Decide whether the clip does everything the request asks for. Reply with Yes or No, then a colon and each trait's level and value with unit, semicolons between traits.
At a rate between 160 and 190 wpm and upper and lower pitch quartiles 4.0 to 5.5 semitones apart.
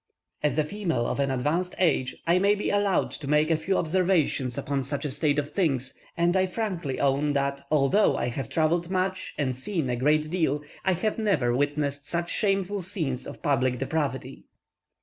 Yes: average, 185 wpm; average, 4.9 semitones